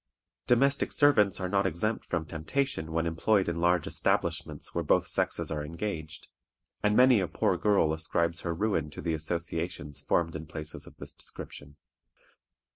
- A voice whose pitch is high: No, very low, 85 Hz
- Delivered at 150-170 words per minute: Yes, average, 160 wpm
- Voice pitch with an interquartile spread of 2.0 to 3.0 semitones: No, average, 4.6 semitones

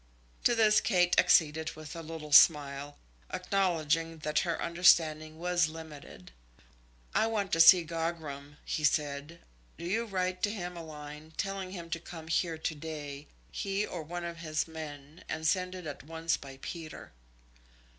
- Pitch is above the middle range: No, medium, 165 Hz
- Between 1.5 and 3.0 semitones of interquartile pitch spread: Yes, narrow, 2.6 semitones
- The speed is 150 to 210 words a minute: Yes, average, 160 wpm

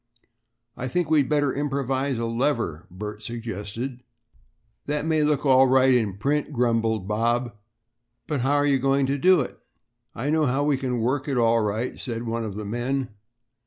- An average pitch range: Yes, average, 3.6 semitones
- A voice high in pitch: No, low, 130 Hz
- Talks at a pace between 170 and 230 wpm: Yes, average, 175 wpm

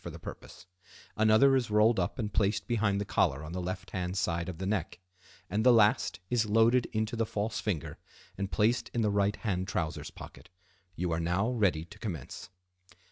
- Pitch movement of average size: Yes, average, 3.3 semitones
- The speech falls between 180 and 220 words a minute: Yes, average, 195 wpm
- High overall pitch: No, low, 100 Hz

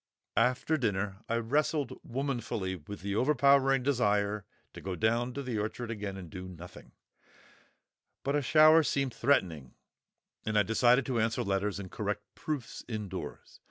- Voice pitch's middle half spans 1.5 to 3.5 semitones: No, average, 5.3 semitones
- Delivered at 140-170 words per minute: Yes, average, 145 wpm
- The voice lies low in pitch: Yes, low, 115 Hz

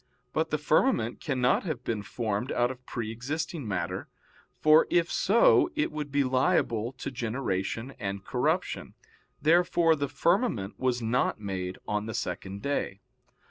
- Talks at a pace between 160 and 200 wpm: No, average, 145 wpm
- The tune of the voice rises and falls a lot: Yes, wide, 6.3 semitones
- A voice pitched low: Yes, low, 125 Hz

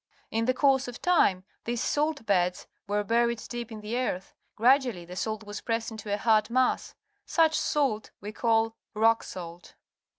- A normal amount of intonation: Yes, average, 3.1 semitones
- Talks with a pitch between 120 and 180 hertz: No, high, 225 Hz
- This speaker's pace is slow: No, average, 170 wpm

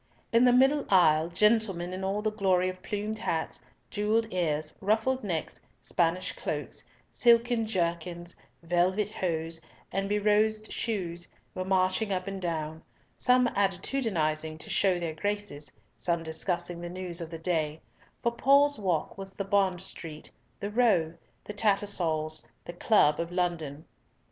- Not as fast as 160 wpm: Yes, average, 145 wpm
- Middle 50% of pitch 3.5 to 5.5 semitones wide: Yes, average, 3.9 semitones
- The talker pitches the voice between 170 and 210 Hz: Yes, medium, 185 Hz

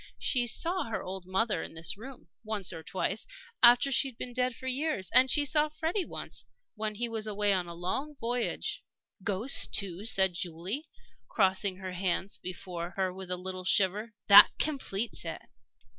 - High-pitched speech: Yes, high, 205 Hz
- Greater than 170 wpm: Yes, average, 180 wpm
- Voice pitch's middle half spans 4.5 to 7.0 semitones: Yes, average, 5.2 semitones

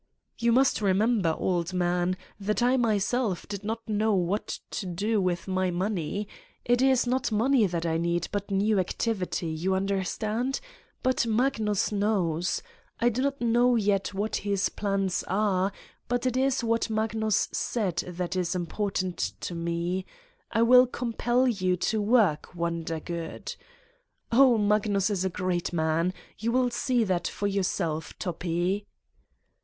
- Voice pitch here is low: No, high, 200 Hz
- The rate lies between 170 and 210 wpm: No, average, 150 wpm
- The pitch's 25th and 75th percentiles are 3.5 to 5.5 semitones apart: Yes, average, 4.2 semitones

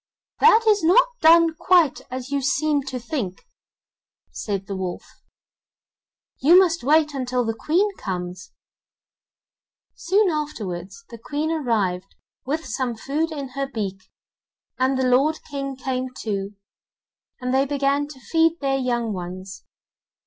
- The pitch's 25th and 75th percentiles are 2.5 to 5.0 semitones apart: No, wide, 5.6 semitones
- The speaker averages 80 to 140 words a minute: Yes, slow, 135 wpm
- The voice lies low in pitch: No, very high, 270 Hz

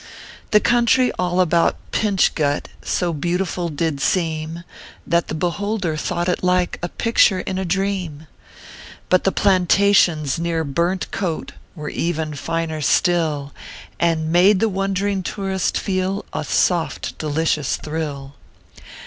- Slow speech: Yes, slow, 130 wpm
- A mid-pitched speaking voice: Yes, medium, 175 Hz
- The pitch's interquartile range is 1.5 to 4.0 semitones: Yes, average, 3.3 semitones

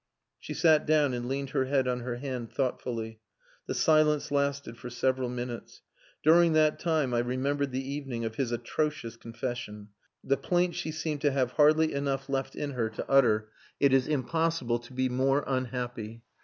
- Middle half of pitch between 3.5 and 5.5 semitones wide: No, average, 3.1 semitones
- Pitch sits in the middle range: No, low, 130 Hz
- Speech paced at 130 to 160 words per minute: No, average, 180 wpm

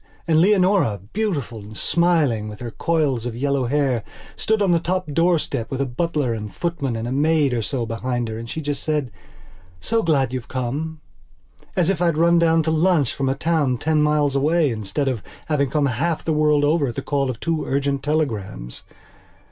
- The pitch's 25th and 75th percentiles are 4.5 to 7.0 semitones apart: Yes, average, 4.8 semitones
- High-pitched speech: No, medium, 145 Hz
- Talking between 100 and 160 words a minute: No, average, 195 wpm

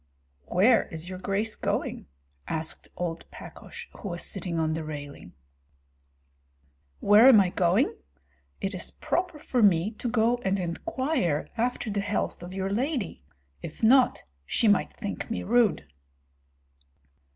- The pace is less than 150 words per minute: Yes, average, 140 wpm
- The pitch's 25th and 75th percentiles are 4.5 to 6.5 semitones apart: Yes, average, 5.3 semitones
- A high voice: Yes, high, 200 Hz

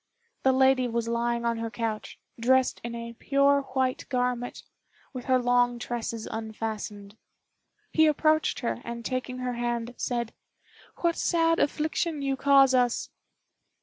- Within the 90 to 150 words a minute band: Yes, average, 140 wpm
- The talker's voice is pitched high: Yes, high, 245 Hz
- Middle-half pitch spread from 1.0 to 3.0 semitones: Yes, narrow, 2.4 semitones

